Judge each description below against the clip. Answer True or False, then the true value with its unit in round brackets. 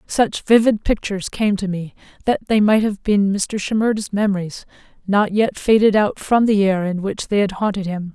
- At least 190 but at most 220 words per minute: True (200 wpm)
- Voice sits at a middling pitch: False (205 Hz)